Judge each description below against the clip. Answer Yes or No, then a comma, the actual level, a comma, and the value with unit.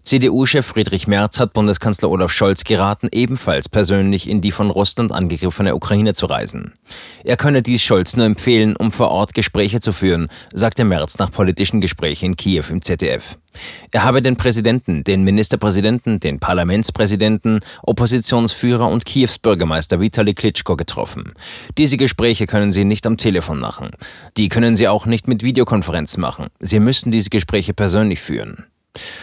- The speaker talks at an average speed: Yes, average, 155 wpm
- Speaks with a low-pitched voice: Yes, low, 105 Hz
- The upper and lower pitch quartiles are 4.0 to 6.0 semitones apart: No, average, 3.2 semitones